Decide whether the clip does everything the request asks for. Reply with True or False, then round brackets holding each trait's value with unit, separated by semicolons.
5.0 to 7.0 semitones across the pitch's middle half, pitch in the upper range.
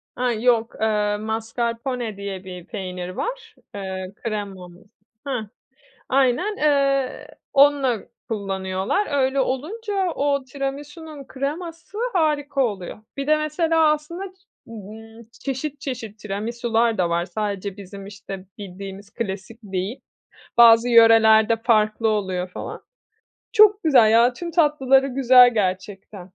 True (5.6 semitones; 230 Hz)